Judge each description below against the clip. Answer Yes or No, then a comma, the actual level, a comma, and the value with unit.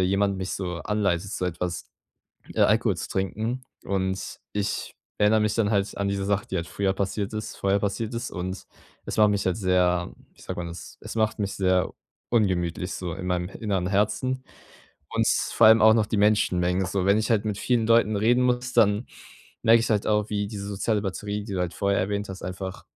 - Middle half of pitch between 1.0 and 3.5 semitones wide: Yes, narrow, 2.5 semitones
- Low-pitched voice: Yes, low, 100 Hz